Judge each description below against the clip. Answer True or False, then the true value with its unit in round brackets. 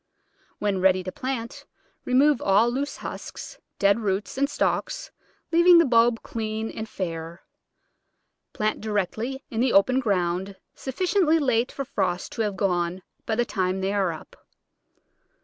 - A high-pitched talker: True (220 Hz)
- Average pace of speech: True (145 wpm)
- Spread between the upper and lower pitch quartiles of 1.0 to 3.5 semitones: False (5.1 semitones)